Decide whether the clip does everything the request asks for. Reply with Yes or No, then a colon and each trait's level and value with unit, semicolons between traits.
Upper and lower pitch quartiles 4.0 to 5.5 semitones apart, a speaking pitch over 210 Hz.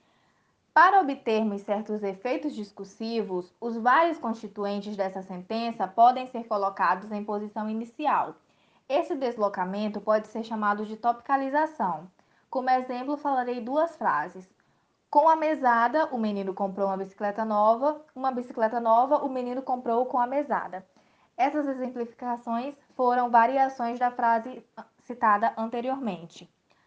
No: average, 3.6 semitones; high, 235 Hz